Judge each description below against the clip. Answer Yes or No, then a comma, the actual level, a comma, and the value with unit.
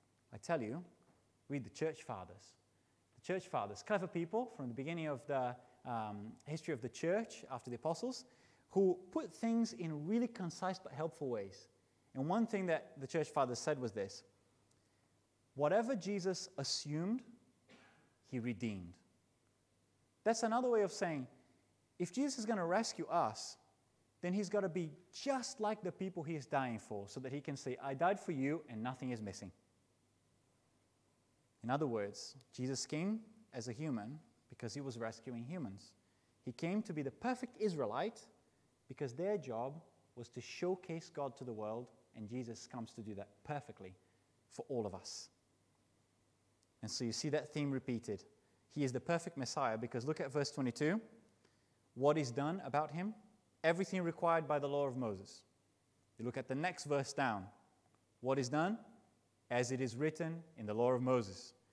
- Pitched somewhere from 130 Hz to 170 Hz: Yes, low, 135 Hz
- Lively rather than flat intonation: Yes, wide, 6.5 semitones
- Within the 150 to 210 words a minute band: Yes, average, 170 wpm